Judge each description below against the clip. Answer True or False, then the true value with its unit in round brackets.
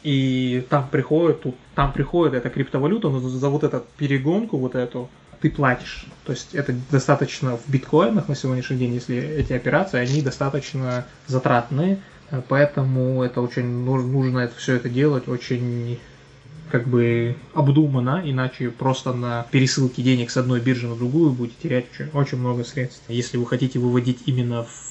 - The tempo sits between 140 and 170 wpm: True (160 wpm)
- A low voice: True (130 Hz)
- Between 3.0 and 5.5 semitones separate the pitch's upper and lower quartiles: False (2.4 semitones)